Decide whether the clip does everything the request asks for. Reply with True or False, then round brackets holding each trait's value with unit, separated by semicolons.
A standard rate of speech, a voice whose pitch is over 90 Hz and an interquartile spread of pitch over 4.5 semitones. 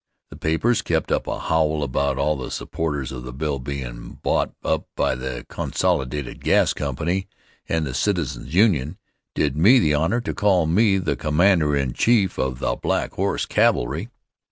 False (170 wpm; 75 Hz; 5.1 semitones)